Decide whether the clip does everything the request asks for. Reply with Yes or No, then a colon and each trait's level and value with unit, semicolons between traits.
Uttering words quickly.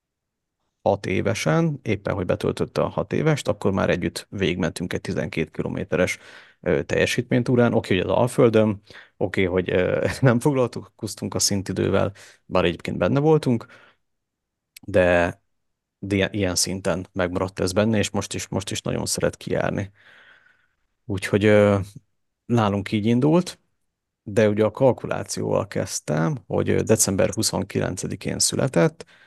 No: average, 125 wpm